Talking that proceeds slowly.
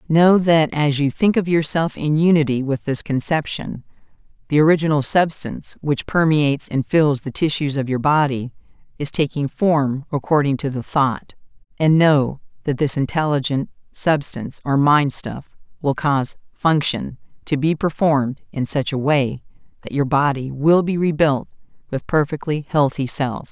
No: average, 155 wpm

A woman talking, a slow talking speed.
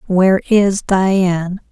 Yes: female; slow, 105 wpm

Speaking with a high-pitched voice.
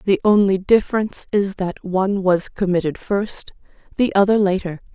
Yes: high, 195 Hz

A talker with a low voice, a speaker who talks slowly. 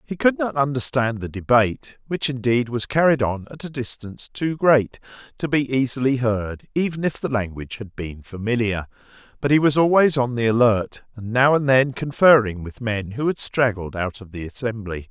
No: low, 125 Hz; average, 190 wpm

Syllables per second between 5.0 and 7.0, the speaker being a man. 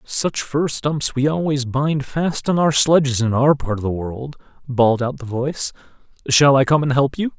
No: 4.7 syllables/s; male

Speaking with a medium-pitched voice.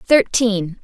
No: high, 215 Hz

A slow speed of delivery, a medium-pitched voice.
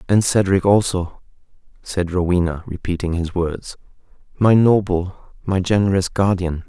No: slow, 110 wpm; very low, 90 Hz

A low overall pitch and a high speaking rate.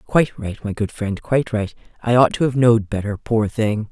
Yes: low, 110 Hz; fast, 230 wpm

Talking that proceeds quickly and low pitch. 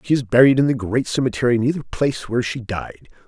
Yes: fast, 240 wpm; low, 120 Hz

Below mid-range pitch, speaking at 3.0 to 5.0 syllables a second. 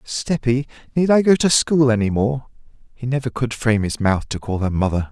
No: low, 125 Hz; 5.3 syllables/s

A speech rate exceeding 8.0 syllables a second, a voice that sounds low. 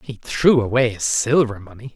No: 5.0 syllables/s; low, 120 Hz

